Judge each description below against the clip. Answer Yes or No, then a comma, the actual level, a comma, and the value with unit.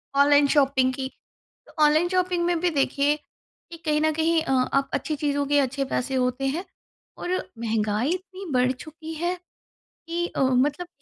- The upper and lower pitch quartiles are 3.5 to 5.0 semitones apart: Yes, average, 3.8 semitones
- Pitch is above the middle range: Yes, very high, 290 Hz